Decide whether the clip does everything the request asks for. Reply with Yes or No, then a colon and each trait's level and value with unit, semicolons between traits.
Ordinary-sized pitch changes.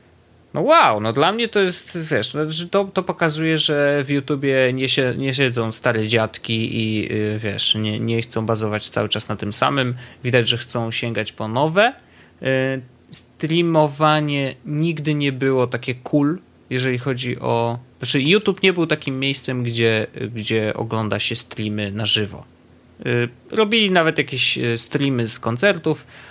Yes: average, 4.8 semitones